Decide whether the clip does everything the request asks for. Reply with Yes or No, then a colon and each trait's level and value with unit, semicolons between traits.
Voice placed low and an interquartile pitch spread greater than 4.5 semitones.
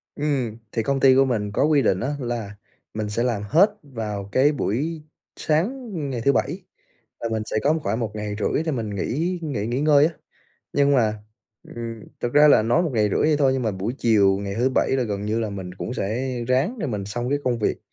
Yes: low, 120 Hz; average, 5.1 semitones